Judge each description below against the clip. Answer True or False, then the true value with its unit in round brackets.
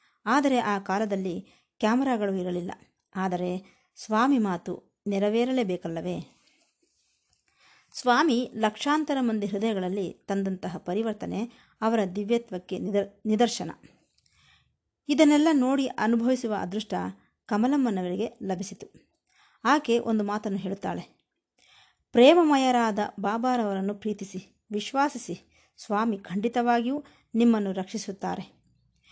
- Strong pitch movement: False (3.9 semitones)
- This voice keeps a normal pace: True (75 wpm)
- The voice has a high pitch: True (215 Hz)